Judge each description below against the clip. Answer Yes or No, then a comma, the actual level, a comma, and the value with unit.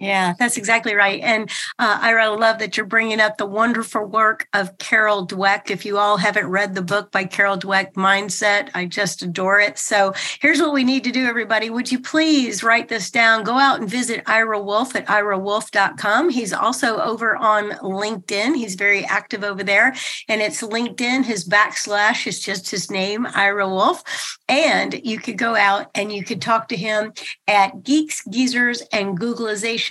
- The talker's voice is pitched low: No, high, 215 Hz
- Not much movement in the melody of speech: Yes, narrow, 2.3 semitones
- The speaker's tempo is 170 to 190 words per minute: Yes, average, 185 wpm